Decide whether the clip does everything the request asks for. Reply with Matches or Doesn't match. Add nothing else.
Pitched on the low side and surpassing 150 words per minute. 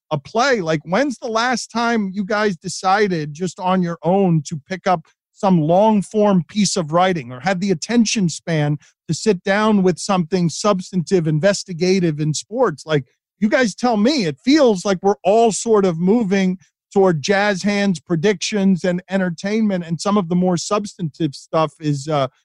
Doesn't match